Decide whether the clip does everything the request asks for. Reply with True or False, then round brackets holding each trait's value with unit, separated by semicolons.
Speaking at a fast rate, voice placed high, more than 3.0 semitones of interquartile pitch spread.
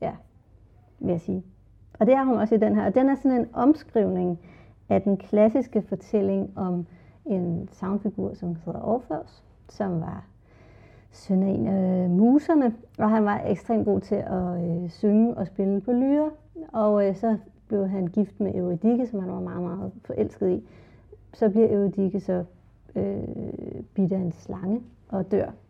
False (175 wpm; 195 Hz; 3.6 semitones)